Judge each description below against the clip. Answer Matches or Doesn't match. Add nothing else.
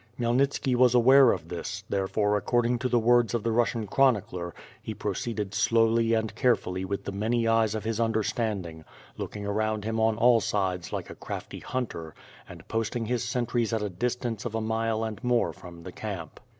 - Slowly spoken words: Doesn't match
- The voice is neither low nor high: Doesn't match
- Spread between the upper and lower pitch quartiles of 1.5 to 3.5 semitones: Matches